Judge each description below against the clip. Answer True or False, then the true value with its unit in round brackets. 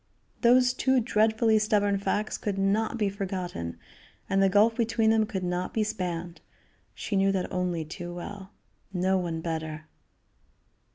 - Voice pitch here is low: False (195 Hz)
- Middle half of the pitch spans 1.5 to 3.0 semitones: False (3.5 semitones)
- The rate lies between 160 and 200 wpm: False (150 wpm)